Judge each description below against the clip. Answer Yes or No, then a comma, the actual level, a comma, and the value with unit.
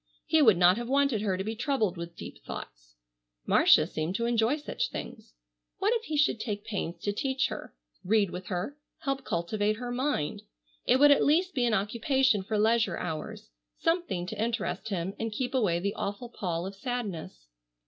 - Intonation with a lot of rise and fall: Yes, wide, 6.0 semitones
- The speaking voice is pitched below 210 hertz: No, high, 220 Hz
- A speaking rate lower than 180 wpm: No, average, 190 wpm